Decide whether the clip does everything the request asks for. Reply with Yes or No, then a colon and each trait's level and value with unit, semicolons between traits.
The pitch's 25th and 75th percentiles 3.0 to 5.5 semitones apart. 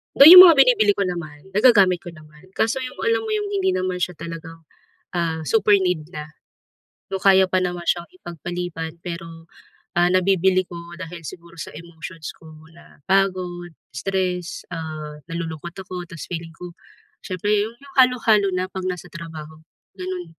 No: narrow, 2.6 semitones